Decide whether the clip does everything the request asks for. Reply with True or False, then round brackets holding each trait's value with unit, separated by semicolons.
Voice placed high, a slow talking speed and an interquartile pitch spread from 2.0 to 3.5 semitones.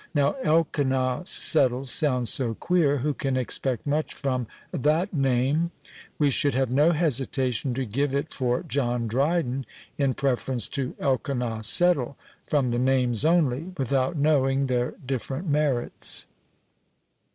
False (135 Hz; 130 wpm; 2.9 semitones)